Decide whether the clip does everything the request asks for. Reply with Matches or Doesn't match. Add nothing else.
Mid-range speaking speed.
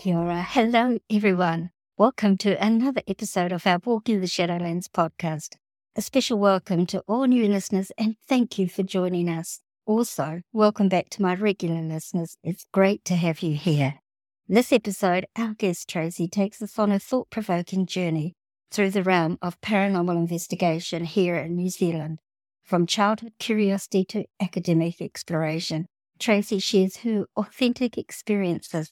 Matches